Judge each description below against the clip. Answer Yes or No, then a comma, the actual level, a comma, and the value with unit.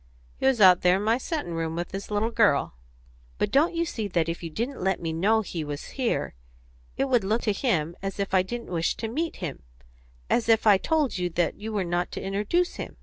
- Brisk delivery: Yes, fast, 240 wpm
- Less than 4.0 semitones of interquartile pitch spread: No, average, 5.2 semitones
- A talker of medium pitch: No, high, 200 Hz